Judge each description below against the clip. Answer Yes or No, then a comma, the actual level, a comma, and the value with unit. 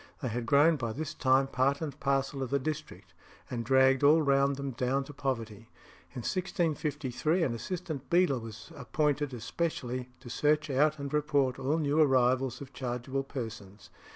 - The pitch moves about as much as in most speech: Yes, average, 3.0 semitones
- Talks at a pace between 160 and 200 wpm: Yes, average, 165 wpm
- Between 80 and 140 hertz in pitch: Yes, low, 135 Hz